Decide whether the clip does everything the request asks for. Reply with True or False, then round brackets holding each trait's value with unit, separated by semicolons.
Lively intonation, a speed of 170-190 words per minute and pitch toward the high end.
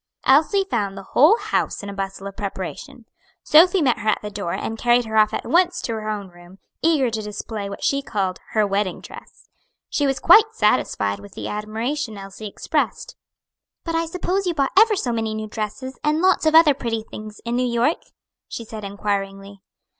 False (6.5 semitones; 200 wpm; 225 Hz)